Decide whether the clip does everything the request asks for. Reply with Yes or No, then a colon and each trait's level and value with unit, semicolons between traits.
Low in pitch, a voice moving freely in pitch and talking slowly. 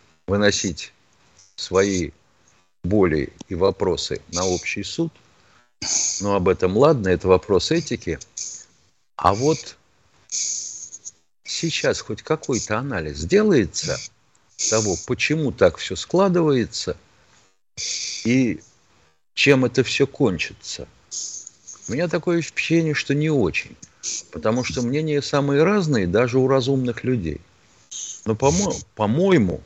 Yes: low, 115 Hz; wide, 7.4 semitones; slow, 105 wpm